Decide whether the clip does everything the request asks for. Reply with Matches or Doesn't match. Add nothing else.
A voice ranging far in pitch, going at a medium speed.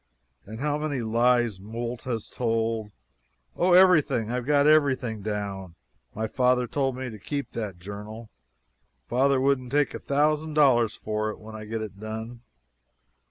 Doesn't match